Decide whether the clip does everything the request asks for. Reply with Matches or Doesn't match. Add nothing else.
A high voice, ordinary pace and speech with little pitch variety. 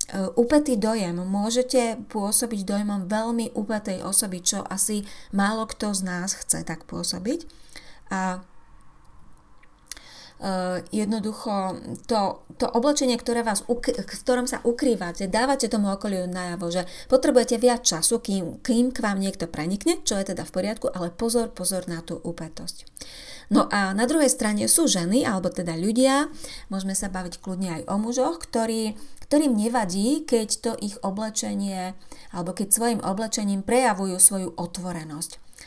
Doesn't match